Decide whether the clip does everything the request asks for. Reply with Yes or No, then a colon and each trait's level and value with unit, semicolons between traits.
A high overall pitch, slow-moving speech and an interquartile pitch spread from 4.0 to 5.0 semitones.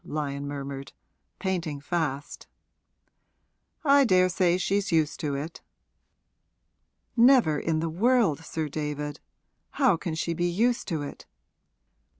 No: medium, 165 Hz; slow, 115 wpm; average, 4.4 semitones